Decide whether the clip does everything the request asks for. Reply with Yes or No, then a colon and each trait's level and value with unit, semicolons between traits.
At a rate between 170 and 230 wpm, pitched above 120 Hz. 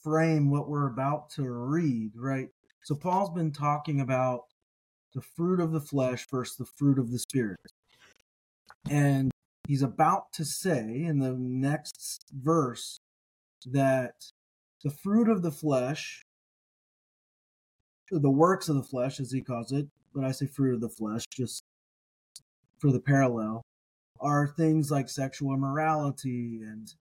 No: average, 140 wpm; low, 135 Hz